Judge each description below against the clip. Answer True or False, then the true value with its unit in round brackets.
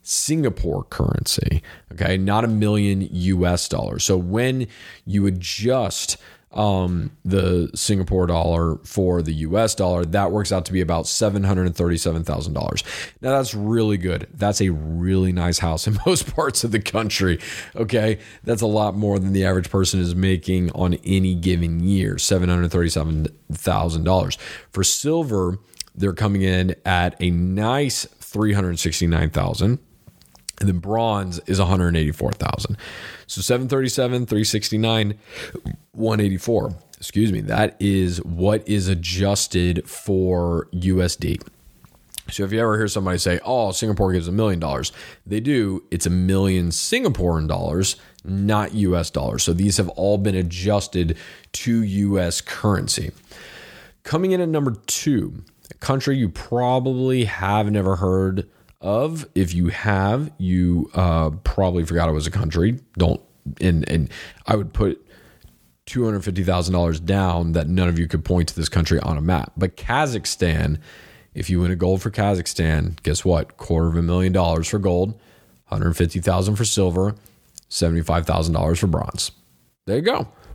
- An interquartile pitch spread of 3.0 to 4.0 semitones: True (3.3 semitones)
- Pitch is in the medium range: False (95 Hz)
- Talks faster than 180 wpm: False (140 wpm)